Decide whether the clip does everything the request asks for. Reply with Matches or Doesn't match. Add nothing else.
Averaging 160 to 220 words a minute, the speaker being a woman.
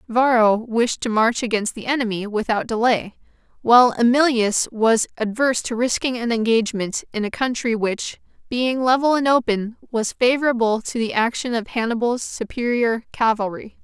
Doesn't match